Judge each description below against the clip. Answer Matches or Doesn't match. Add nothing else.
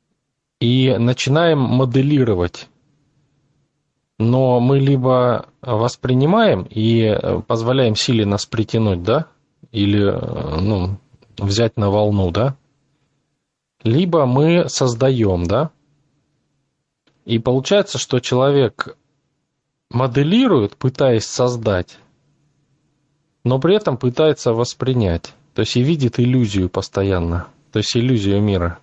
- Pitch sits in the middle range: Doesn't match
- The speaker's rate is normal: Doesn't match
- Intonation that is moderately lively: Matches